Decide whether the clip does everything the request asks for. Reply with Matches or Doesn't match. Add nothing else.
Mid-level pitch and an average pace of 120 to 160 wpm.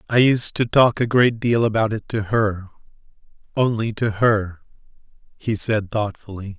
Doesn't match